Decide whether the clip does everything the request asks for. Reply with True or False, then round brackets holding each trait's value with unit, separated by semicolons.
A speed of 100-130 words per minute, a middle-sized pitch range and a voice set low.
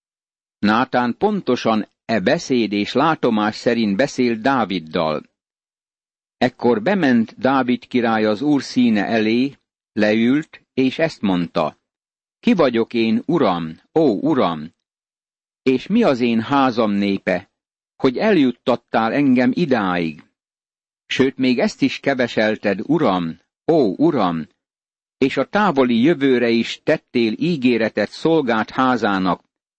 True (110 wpm; 4.1 semitones; 120 Hz)